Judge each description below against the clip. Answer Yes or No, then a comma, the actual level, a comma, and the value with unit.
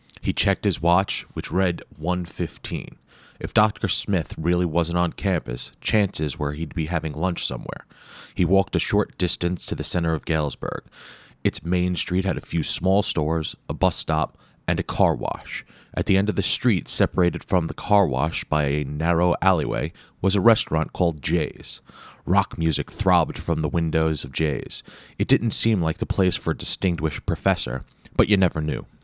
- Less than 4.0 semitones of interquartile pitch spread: Yes, average, 3.4 semitones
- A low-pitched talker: Yes, very low, 90 Hz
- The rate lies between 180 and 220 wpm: Yes, average, 185 wpm